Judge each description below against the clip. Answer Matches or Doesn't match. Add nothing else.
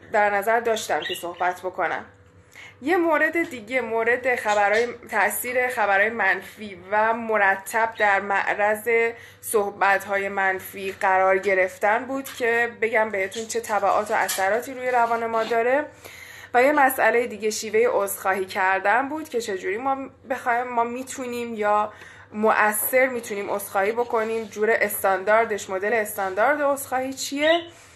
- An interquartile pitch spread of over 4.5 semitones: Doesn't match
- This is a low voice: Doesn't match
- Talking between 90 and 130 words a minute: Matches